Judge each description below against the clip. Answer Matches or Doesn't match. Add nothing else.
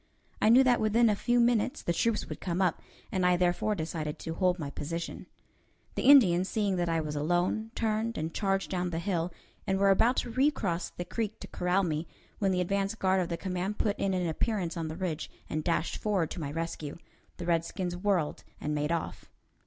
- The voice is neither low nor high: Matches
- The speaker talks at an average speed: Doesn't match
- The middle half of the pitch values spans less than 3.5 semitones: Doesn't match